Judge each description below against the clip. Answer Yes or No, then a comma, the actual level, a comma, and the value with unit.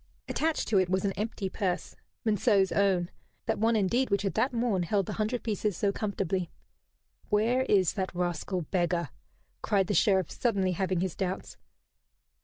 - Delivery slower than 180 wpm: Yes, average, 165 wpm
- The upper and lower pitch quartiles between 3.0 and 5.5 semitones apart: No, narrow, 2.5 semitones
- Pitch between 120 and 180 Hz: No, high, 195 Hz